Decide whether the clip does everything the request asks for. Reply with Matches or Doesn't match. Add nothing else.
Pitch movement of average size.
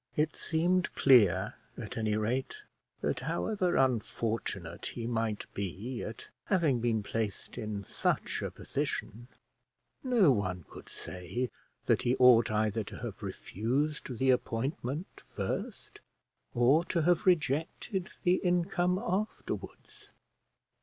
Doesn't match